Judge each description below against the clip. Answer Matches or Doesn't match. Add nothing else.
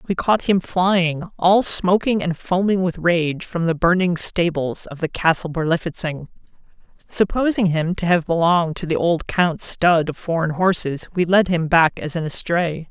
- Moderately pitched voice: Matches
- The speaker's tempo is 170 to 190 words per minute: Matches